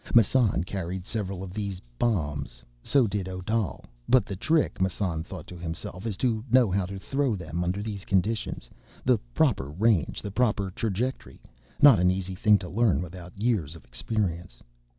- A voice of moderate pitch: No, very low, 95 Hz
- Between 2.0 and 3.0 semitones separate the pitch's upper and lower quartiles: No, average, 3.8 semitones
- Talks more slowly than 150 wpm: No, average, 170 wpm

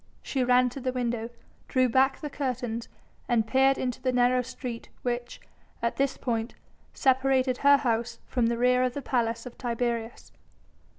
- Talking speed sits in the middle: Yes, average, 165 wpm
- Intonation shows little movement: Yes, narrow, 1.7 semitones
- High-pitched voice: Yes, very high, 250 Hz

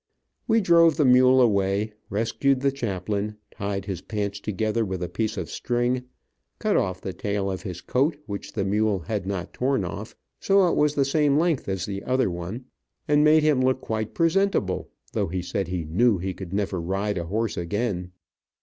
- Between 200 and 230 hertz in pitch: No, low, 105 Hz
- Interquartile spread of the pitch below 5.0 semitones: No, average, 5.3 semitones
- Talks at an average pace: Yes, average, 190 wpm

